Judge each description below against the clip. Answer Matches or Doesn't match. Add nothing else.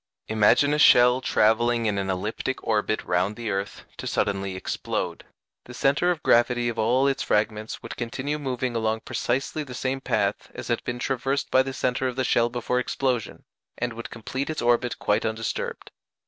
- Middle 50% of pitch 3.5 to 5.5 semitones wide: Doesn't match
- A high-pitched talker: Doesn't match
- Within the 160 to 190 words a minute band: Matches